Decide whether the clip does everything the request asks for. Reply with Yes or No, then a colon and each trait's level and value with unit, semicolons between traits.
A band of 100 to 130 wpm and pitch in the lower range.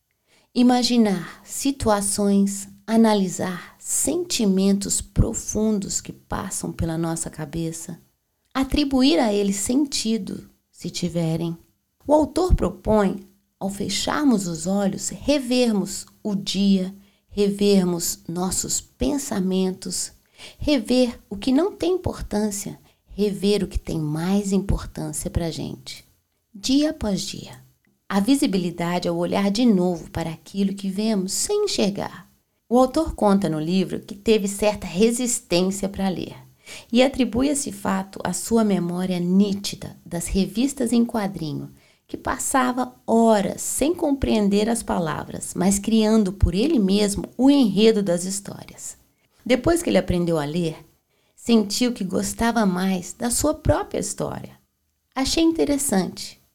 No: slow, 120 wpm; high, 200 Hz